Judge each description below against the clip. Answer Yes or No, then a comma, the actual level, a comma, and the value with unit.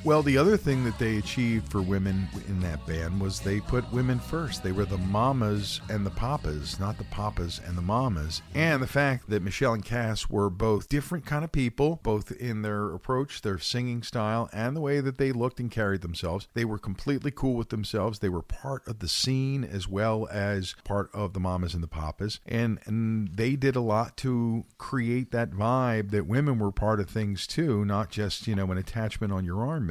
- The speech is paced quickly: Yes, fast, 215 wpm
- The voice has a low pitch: Yes, low, 110 Hz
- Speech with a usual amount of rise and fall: Yes, average, 4.2 semitones